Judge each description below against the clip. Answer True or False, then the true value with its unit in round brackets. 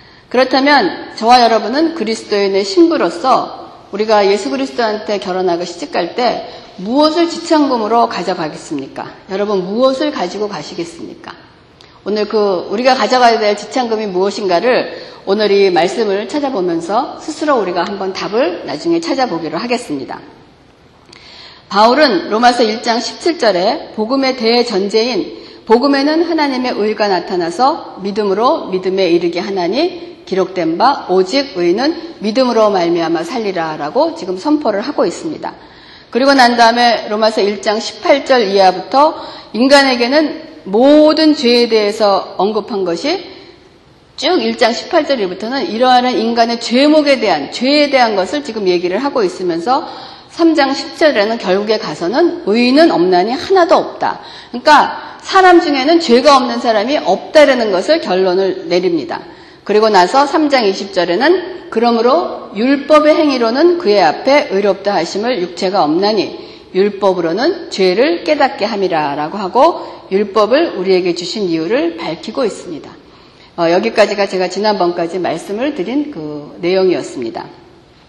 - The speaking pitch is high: True (235 Hz)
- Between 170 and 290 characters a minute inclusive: False (320 characters per minute)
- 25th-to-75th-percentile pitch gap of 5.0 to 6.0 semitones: False (7.6 semitones)